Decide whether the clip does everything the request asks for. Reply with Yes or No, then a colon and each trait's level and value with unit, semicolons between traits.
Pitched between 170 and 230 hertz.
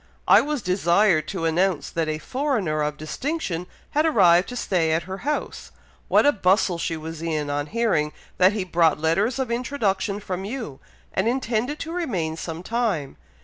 Yes: medium, 185 Hz